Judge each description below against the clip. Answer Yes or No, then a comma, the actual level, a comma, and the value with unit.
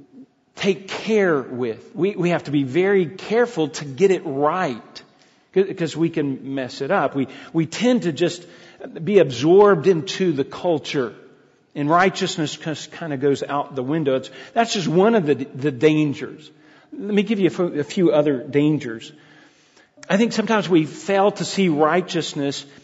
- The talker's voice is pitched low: No, medium, 165 Hz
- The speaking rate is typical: Yes, average, 165 wpm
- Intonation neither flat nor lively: Yes, average, 5.0 semitones